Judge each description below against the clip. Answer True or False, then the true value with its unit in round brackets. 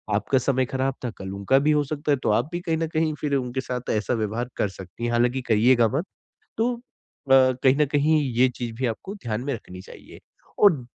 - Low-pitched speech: True (130 Hz)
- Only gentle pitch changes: False (4.0 semitones)